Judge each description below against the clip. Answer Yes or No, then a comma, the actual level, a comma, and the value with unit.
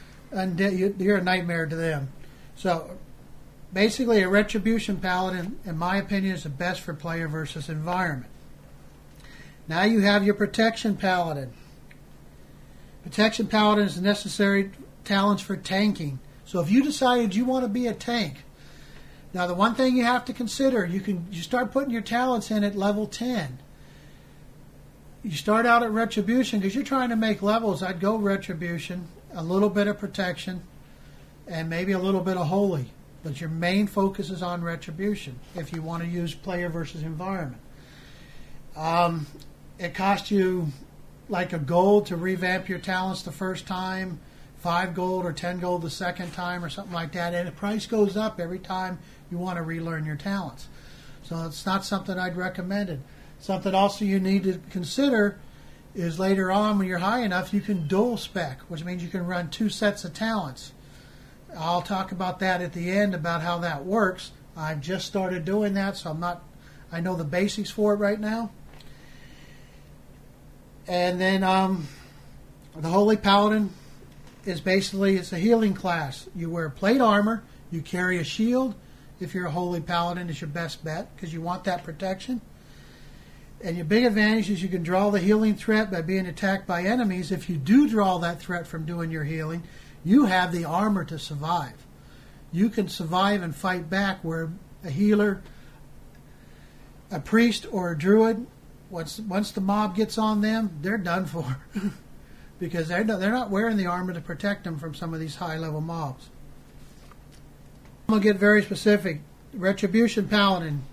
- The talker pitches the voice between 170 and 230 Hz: Yes, medium, 185 Hz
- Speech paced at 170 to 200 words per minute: Yes, average, 175 wpm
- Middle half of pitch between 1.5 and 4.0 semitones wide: Yes, average, 3.5 semitones